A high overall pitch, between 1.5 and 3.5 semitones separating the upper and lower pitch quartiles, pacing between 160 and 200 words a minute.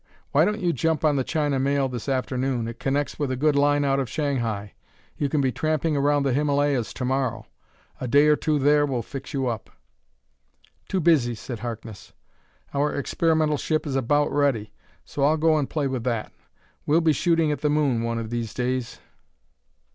No: medium, 140 Hz; average, 3.0 semitones; average, 195 wpm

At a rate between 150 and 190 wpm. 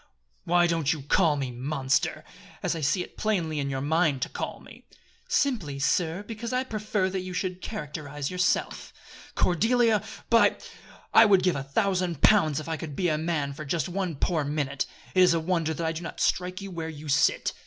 No: average, 200 wpm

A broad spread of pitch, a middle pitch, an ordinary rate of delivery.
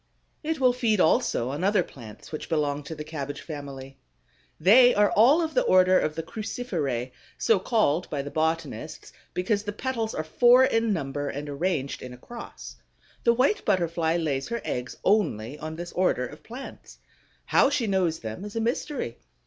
Yes: wide, 7.8 semitones; medium, 170 Hz; average, 180 wpm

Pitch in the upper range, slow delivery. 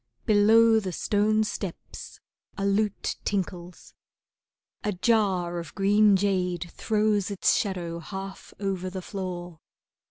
Yes: high, 195 Hz; slow, 115 wpm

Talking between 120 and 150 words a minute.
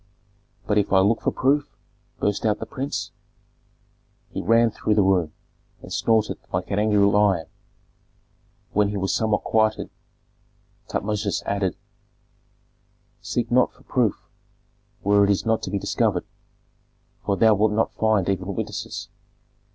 Yes: average, 140 wpm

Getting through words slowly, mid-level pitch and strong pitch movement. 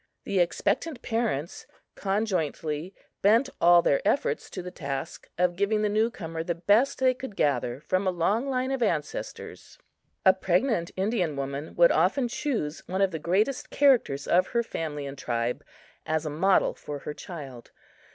No: average, 165 wpm; medium, 180 Hz; wide, 6.3 semitones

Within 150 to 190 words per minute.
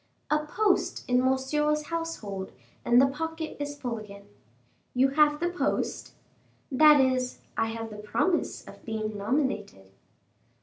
No: slow, 135 wpm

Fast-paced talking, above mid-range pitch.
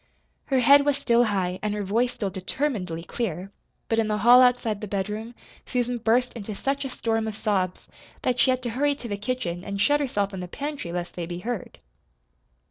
Yes: fast, 210 wpm; high, 225 Hz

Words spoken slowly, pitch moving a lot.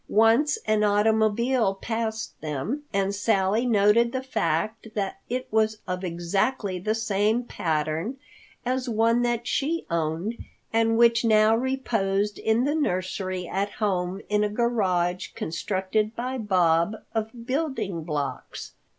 No: slow, 130 wpm; average, 3.8 semitones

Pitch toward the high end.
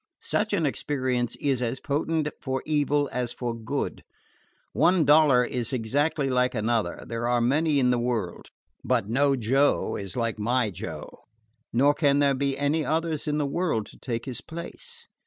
No: low, 135 Hz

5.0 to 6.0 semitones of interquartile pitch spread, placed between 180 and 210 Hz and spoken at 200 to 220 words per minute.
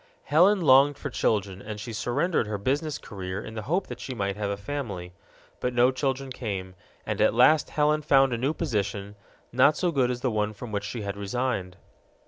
No: average, 5.3 semitones; low, 120 Hz; fast, 205 wpm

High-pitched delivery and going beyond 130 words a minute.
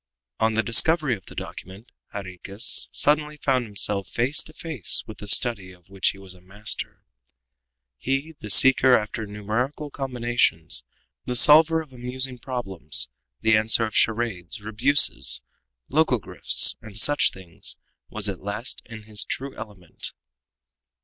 No: low, 110 Hz; average, 140 wpm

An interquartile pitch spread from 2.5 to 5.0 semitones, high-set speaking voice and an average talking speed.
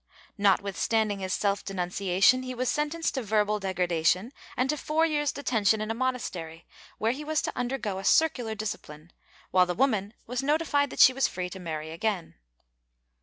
No: wide, 5.6 semitones; high, 215 Hz; average, 180 wpm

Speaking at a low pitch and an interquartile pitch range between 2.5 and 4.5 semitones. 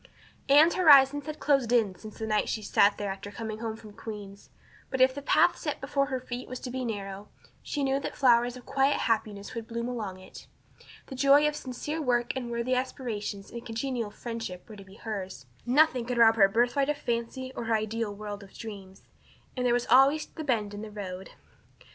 No: high, 235 Hz; average, 4.1 semitones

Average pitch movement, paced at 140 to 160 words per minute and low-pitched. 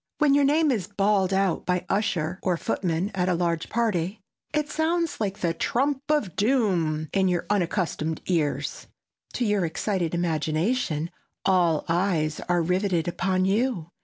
No: average, 4.2 semitones; average, 150 wpm; medium, 185 Hz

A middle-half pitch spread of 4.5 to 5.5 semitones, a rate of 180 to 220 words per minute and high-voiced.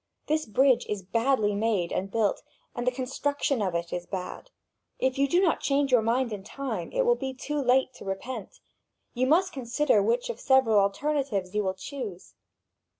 Yes: average, 5.2 semitones; average, 185 wpm; very high, 250 Hz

